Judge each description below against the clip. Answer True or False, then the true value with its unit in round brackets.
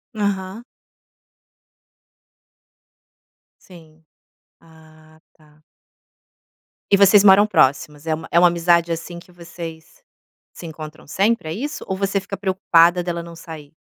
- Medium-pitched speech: True (170 Hz)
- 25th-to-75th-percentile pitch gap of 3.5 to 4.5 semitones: False (3.1 semitones)